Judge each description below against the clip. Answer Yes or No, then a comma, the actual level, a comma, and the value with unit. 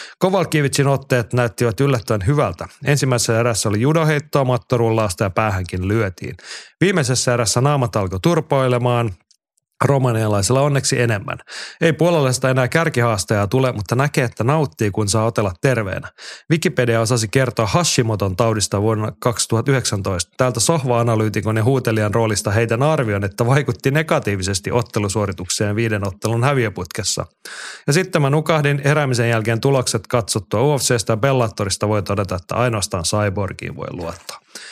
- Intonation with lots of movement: No, average, 4.2 semitones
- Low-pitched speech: Yes, low, 120 Hz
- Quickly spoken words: No, average, 125 wpm